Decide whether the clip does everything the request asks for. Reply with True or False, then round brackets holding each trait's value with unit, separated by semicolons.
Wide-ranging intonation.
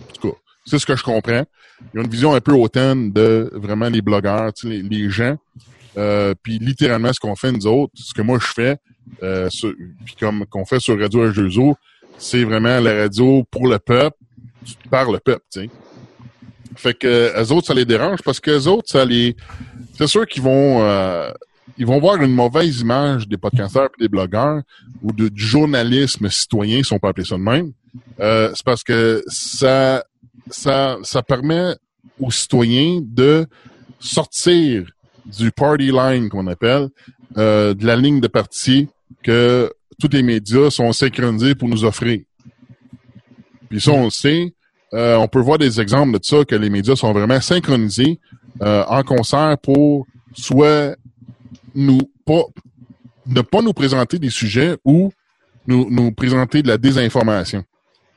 False (3.3 semitones)